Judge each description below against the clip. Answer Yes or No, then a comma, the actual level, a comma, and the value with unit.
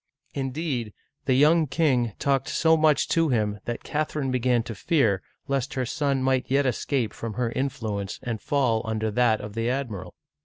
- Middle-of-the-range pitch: No, low, 130 Hz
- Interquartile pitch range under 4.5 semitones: Yes, average, 3.8 semitones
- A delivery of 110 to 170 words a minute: No, average, 185 wpm